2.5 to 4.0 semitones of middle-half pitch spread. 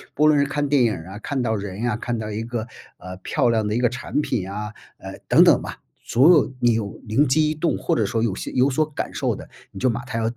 No: average, 4.5 semitones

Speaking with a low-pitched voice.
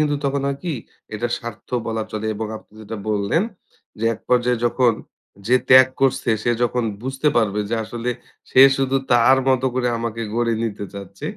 Yes: low, 120 Hz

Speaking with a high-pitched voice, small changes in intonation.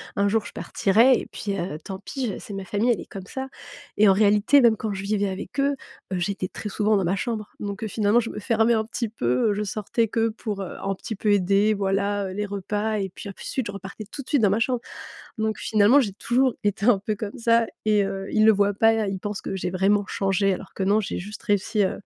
Yes: high, 205 Hz; narrow, 2.1 semitones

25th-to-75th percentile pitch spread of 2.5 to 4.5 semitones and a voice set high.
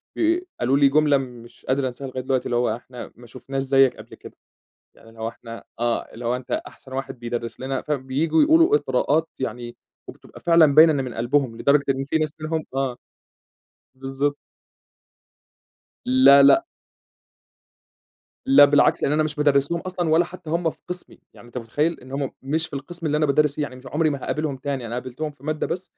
No: average, 3.3 semitones; medium, 140 Hz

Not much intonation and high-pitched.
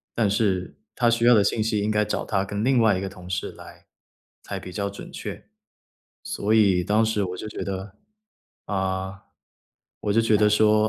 No: narrow, 2.2 semitones; low, 105 Hz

